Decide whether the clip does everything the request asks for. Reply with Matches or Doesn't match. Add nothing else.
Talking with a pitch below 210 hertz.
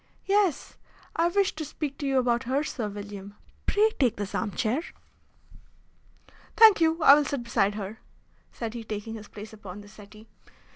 Doesn't match